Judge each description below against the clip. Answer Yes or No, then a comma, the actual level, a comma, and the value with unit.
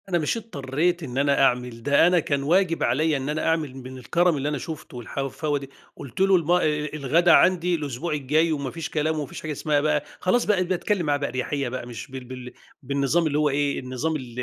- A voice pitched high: No, medium, 150 Hz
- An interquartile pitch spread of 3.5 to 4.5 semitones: Yes, average, 3.8 semitones